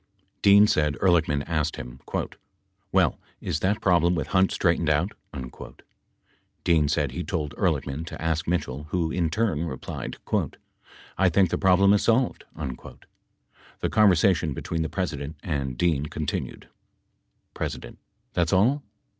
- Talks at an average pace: No, slow, 130 wpm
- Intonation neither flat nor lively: Yes, average, 3.7 semitones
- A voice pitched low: Yes, very low, 85 Hz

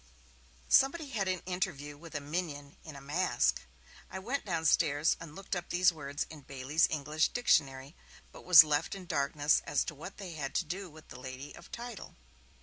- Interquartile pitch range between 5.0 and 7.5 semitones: No, average, 4.2 semitones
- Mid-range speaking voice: Yes, medium, 160 Hz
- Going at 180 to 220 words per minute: Yes, average, 185 wpm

